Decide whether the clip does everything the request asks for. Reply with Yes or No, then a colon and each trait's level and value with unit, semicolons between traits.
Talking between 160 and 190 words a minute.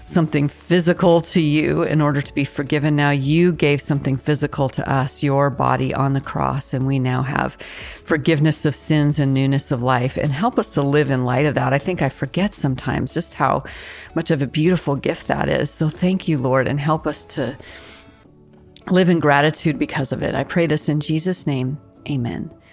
No: average, 200 wpm